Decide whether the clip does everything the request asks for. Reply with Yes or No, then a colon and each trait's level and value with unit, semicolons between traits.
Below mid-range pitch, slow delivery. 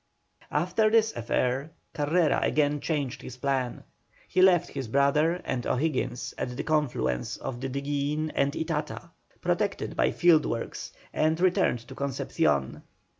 No: medium, 145 Hz; slow, 130 wpm